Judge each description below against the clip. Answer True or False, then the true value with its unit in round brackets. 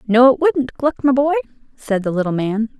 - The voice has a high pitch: True (245 Hz)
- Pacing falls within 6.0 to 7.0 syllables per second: False (5.1 syllables/s)